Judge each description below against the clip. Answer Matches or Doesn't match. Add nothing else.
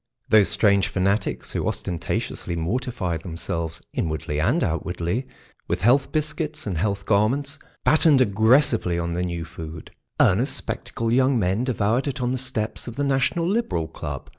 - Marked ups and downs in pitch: Matches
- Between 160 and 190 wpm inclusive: Doesn't match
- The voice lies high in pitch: Doesn't match